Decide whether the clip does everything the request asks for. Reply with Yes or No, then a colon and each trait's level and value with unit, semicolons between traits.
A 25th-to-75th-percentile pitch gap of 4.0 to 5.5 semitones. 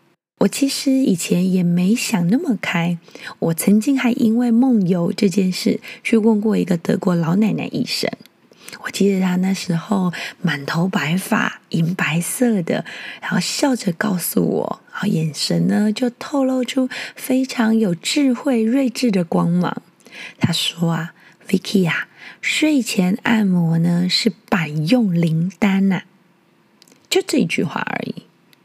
Yes: average, 5.2 semitones